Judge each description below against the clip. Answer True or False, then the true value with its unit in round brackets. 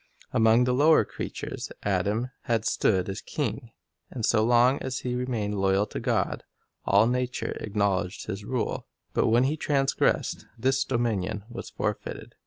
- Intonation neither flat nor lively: True (3.6 semitones)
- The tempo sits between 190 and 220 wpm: False (150 wpm)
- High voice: False (115 Hz)